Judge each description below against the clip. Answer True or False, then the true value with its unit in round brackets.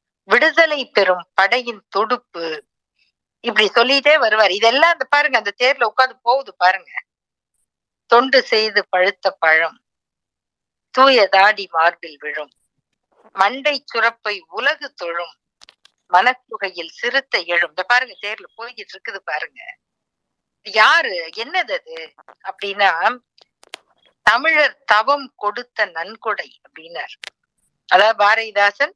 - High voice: True (225 Hz)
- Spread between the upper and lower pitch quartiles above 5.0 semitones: True (5.5 semitones)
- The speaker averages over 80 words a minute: True (95 wpm)